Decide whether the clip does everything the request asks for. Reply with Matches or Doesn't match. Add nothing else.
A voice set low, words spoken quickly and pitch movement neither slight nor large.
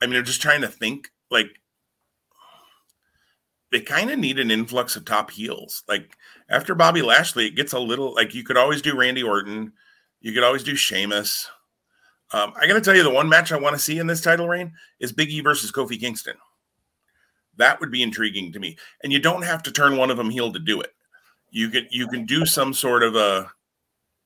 Matches